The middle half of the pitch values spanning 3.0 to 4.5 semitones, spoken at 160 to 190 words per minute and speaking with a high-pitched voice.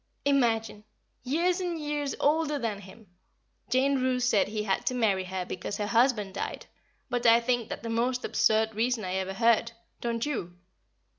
Yes: average, 3.6 semitones; average, 175 wpm; high, 235 Hz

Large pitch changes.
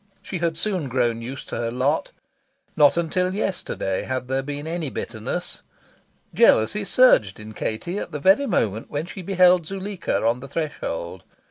Yes: wide, 7.5 semitones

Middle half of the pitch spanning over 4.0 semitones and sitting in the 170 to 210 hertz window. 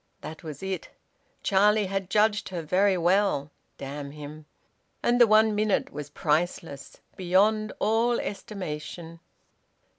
Yes: average, 5.3 semitones; high, 190 Hz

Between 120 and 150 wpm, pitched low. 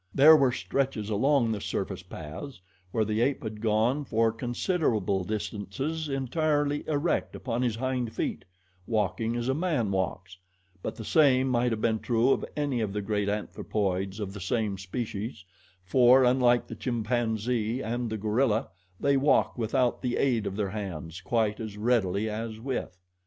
No: average, 160 wpm; low, 115 Hz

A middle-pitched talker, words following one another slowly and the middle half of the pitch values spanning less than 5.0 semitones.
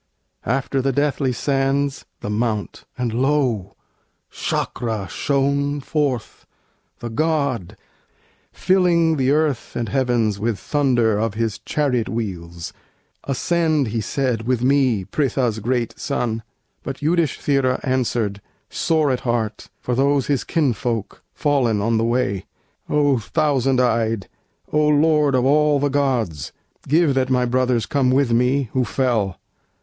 No: low, 130 Hz; slow, 130 wpm; average, 3.8 semitones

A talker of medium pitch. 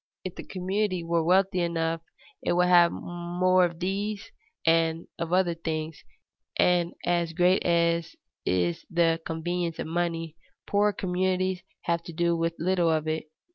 Yes: medium, 170 Hz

